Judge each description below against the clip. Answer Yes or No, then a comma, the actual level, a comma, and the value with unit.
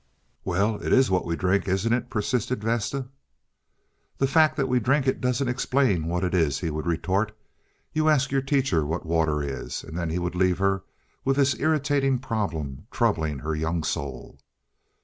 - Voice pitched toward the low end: Yes, low, 100 Hz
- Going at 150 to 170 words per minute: No, average, 180 wpm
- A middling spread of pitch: No, wide, 7.9 semitones